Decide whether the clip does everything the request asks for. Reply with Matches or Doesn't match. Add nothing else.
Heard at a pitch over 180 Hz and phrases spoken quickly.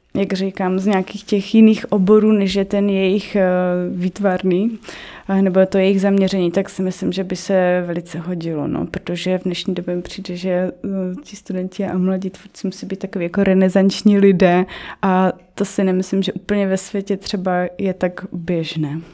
Matches